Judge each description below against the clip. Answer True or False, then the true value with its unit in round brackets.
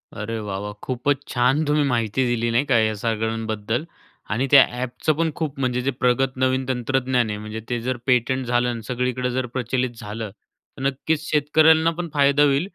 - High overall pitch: False (125 Hz)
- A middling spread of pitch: True (3.1 semitones)